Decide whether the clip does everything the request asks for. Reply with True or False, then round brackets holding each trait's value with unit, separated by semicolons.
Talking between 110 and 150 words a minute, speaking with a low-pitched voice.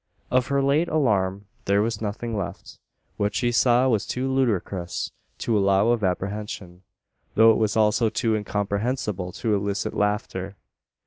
True (145 wpm; 105 Hz)